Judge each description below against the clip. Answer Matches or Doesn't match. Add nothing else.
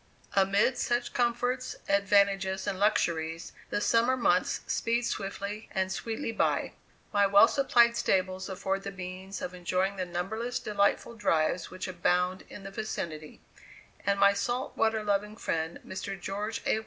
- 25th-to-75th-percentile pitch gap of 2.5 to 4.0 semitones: Matches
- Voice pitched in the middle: Doesn't match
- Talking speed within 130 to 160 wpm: Matches